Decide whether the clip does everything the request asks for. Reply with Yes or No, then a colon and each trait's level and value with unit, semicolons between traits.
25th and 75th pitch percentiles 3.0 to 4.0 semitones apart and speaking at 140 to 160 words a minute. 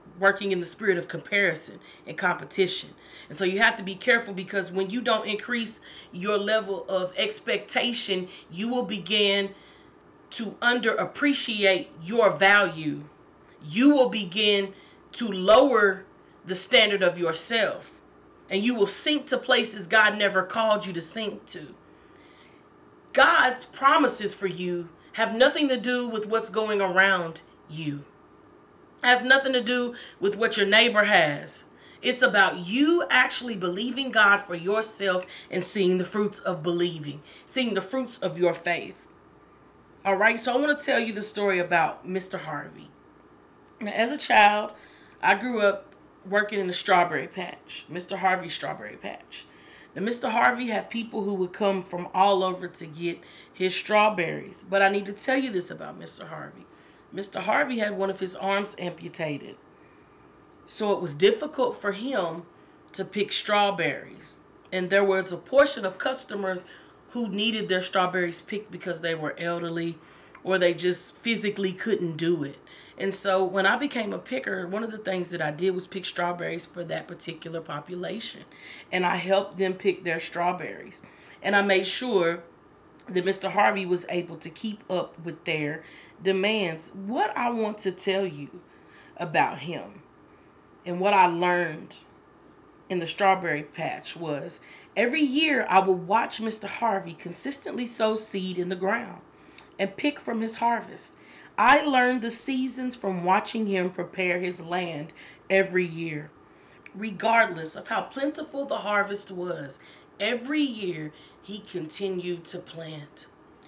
Yes: average, 3.7 semitones; average, 155 wpm